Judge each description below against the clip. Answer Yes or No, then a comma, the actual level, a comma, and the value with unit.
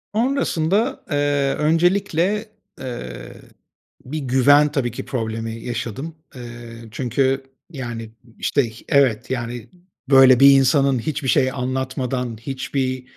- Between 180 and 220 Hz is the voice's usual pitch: No, low, 135 Hz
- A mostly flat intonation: No, average, 3.2 semitones